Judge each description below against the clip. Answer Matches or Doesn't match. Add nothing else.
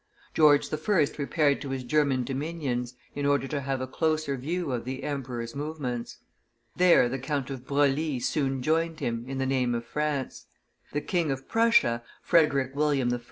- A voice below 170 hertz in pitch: Matches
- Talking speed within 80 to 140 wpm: Doesn't match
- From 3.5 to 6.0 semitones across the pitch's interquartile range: Doesn't match